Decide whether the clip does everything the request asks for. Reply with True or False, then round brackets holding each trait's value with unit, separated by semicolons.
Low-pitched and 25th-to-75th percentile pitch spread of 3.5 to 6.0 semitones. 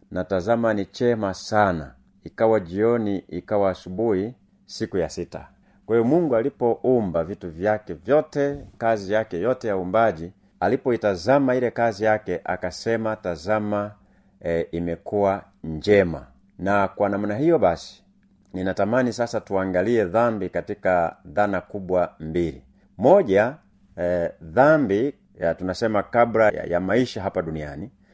True (100 Hz; 4.1 semitones)